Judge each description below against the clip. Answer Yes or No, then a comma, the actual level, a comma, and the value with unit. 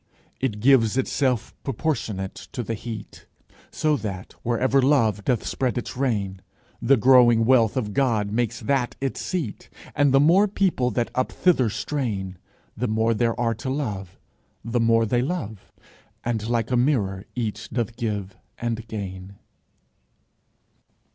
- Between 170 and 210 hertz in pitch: No, low, 120 Hz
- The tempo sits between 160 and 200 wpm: No, average, 145 wpm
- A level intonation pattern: No, average, 3.7 semitones